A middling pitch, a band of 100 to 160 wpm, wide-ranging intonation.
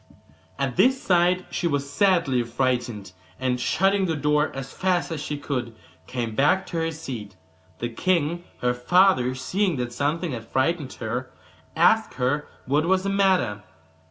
Yes: medium, 145 Hz; average, 155 wpm; wide, 6.0 semitones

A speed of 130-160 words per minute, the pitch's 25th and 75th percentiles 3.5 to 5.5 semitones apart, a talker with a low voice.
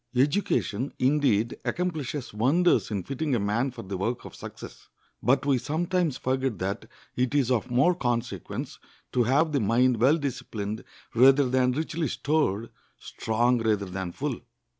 Yes: average, 145 wpm; average, 4.3 semitones; low, 125 Hz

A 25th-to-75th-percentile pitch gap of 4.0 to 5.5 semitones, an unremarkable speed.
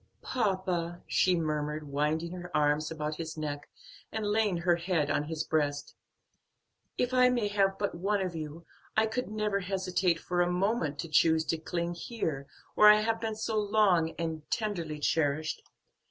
Yes: average, 4.8 semitones; average, 170 wpm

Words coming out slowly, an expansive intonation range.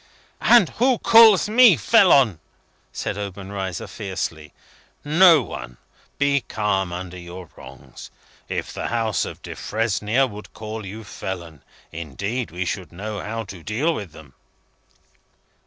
Yes: slow, 125 wpm; wide, 6.4 semitones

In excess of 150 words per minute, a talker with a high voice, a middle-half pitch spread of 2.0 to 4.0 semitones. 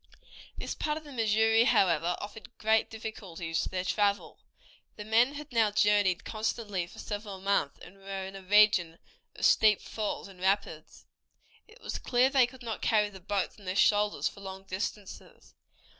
Yes: average, 175 wpm; high, 205 Hz; narrow, 2.6 semitones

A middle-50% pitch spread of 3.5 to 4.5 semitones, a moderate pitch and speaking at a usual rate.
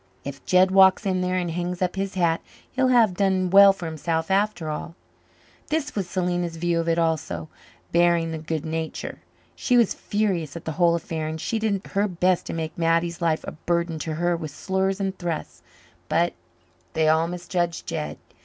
No: narrow, 2.6 semitones; medium, 175 Hz; average, 190 wpm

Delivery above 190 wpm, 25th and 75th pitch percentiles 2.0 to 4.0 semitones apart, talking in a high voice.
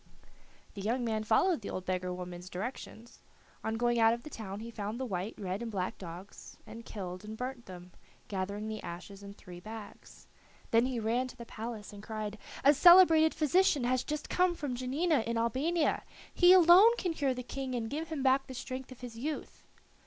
No: average, 200 wpm; average, 4.6 semitones; high, 235 Hz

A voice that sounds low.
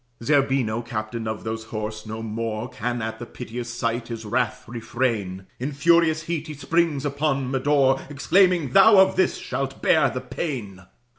Yes: low, 125 Hz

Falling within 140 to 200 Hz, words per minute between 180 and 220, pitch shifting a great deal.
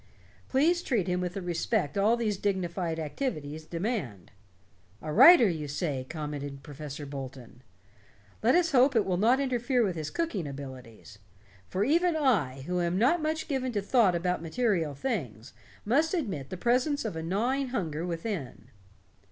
No: medium, 185 Hz; average, 160 wpm; wide, 8.8 semitones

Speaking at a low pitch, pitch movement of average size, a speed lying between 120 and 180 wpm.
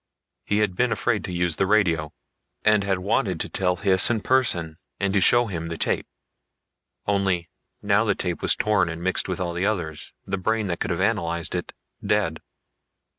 No: very low, 95 Hz; average, 3.3 semitones; average, 190 wpm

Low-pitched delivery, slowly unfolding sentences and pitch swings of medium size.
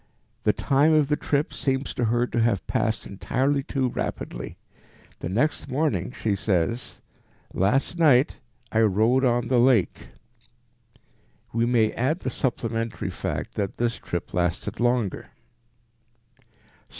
Yes: low, 120 Hz; slow, 130 wpm; average, 3.6 semitones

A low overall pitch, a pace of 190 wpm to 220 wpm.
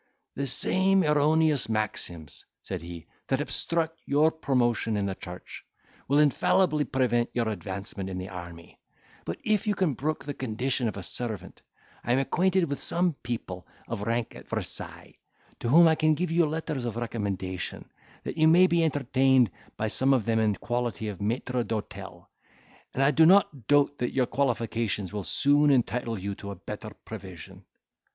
No: low, 125 Hz; average, 175 wpm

